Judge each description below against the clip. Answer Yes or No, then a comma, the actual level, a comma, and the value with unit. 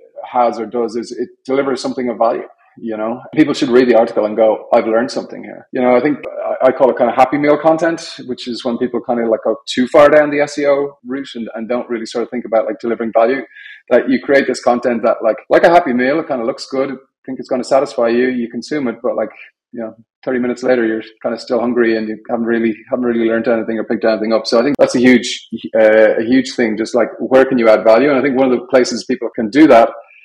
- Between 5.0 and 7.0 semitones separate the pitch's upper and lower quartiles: No, narrow, 2.6 semitones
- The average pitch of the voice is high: No, low, 120 Hz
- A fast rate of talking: Yes, fast, 275 wpm